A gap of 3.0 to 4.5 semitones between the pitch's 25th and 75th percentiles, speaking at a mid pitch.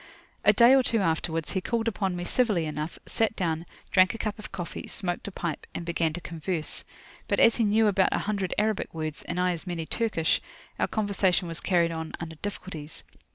Yes: average, 4.2 semitones; medium, 180 Hz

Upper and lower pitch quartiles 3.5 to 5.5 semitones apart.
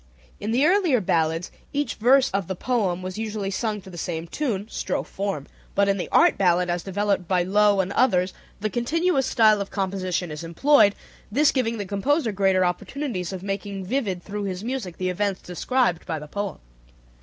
Yes: average, 4.2 semitones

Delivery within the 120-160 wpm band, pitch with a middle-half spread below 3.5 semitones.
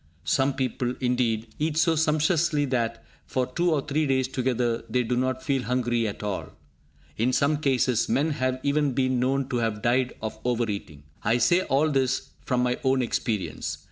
No: average, 180 wpm; average, 2.8 semitones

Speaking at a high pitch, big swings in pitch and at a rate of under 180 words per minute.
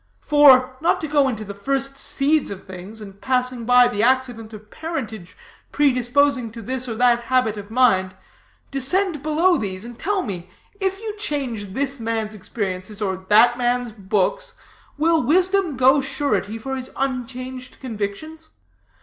No: very high, 250 Hz; average, 4.7 semitones; average, 155 wpm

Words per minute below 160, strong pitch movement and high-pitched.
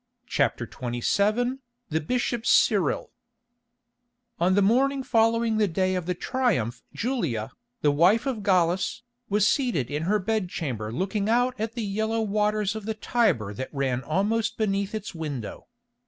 Yes: average, 150 wpm; wide, 5.8 semitones; high, 200 Hz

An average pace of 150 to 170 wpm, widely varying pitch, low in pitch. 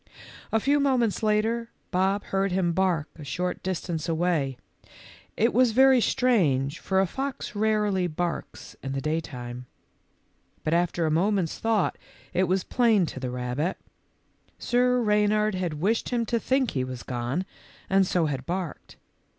No: average, 160 wpm; wide, 5.8 semitones; medium, 185 Hz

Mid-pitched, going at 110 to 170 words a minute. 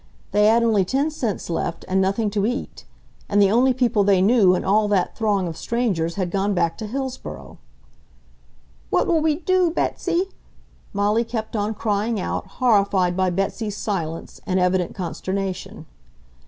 No: high, 205 Hz; average, 160 wpm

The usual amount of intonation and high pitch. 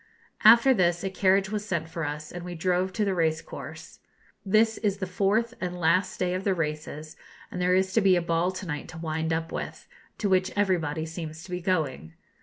No: average, 3.0 semitones; medium, 180 Hz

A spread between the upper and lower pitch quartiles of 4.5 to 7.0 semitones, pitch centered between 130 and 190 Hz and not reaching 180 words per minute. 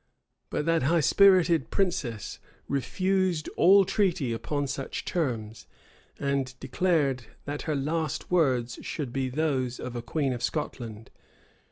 Yes: average, 4.8 semitones; medium, 140 Hz; slow, 135 wpm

